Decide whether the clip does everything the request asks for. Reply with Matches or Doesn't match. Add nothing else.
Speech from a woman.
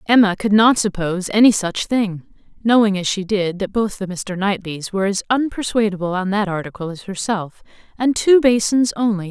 Matches